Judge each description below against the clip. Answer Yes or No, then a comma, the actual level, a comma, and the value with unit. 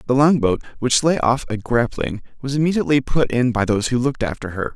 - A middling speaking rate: No, fast, 225 wpm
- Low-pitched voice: Yes, low, 125 Hz